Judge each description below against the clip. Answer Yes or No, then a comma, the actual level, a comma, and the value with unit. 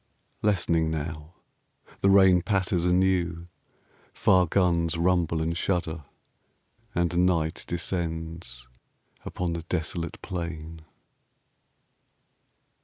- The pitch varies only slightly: Yes, narrow, 1.8 semitones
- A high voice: No, very low, 85 Hz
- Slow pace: Yes, slow, 85 wpm